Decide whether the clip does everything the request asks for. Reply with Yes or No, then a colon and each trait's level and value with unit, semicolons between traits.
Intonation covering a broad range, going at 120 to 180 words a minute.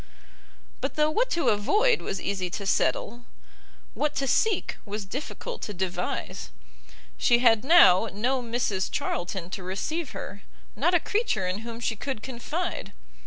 Yes: wide, 7.6 semitones; average, 150 wpm